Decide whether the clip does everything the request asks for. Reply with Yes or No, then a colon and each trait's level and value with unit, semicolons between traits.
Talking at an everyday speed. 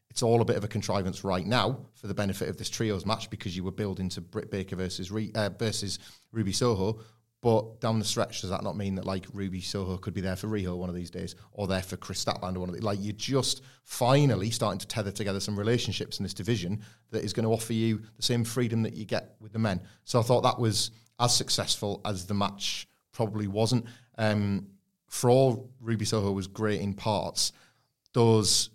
No: fast, 225 wpm